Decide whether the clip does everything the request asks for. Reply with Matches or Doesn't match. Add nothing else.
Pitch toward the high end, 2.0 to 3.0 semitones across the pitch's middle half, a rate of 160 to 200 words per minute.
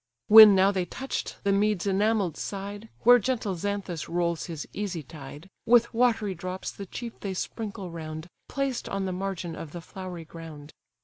Doesn't match